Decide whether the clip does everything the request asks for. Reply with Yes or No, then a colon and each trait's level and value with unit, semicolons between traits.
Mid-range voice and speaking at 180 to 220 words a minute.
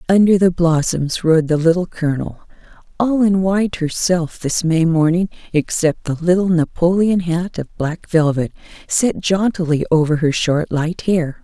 No: medium, 170 Hz; average, 150 wpm